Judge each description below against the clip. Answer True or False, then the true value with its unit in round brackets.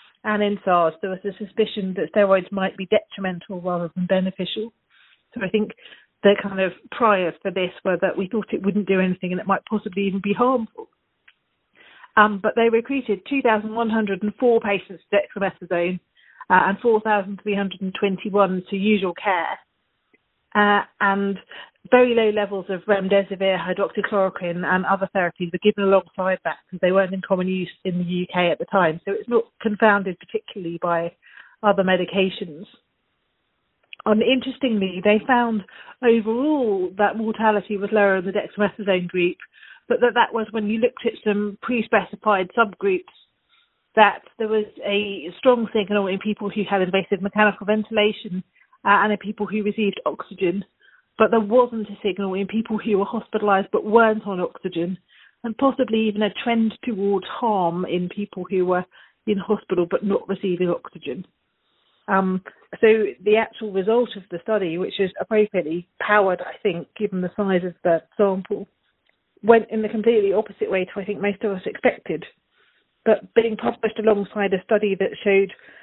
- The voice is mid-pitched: False (205 Hz)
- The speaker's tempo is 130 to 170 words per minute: True (160 wpm)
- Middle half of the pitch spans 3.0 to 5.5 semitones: False (2.4 semitones)